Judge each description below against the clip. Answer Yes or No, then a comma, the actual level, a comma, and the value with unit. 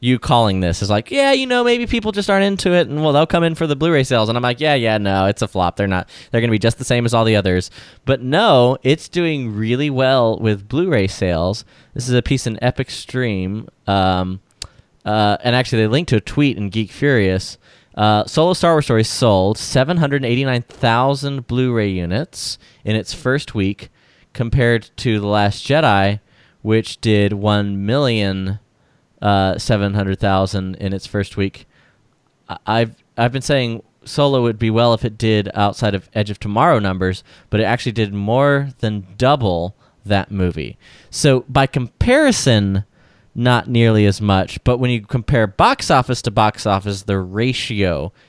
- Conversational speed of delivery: Yes, average, 185 wpm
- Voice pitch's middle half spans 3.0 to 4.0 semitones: No, average, 4.7 semitones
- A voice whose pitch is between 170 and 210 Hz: No, low, 115 Hz